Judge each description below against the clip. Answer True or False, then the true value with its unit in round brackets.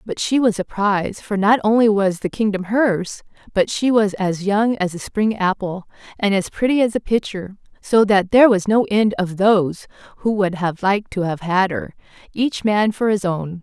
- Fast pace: True (210 wpm)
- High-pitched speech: True (200 Hz)